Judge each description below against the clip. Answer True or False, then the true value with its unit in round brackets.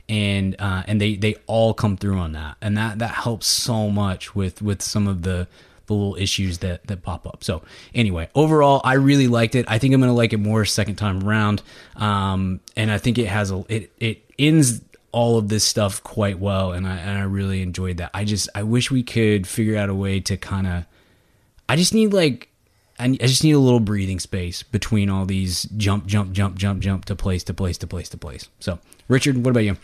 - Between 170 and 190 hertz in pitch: False (105 Hz)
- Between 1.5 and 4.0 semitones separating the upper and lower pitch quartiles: True (2.9 semitones)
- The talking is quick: True (230 wpm)